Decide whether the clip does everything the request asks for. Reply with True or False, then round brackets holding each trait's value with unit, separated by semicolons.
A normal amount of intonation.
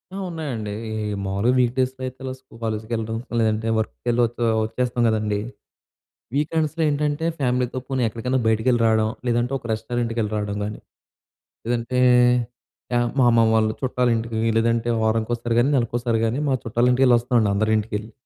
False (2.3 semitones)